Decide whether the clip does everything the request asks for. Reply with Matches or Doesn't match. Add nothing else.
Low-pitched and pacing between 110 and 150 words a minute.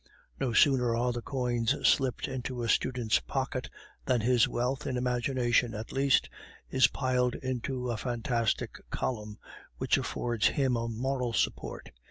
Matches